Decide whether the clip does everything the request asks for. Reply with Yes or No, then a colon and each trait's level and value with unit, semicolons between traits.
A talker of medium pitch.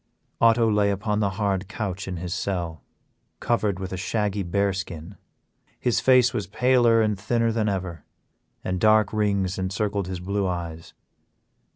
No: low, 100 Hz